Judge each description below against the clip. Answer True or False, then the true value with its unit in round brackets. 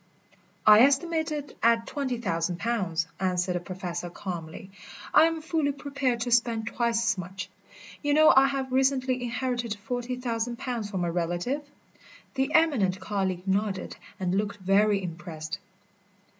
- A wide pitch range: True (6.0 semitones)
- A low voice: False (225 Hz)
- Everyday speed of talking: True (145 wpm)